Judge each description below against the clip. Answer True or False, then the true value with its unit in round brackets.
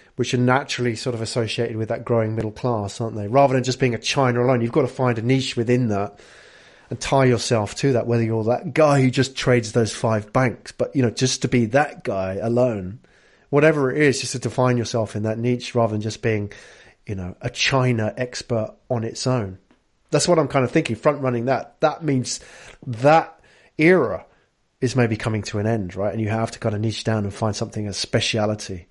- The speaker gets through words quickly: True (220 wpm)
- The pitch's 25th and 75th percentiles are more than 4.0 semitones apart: False (2.9 semitones)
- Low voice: True (120 Hz)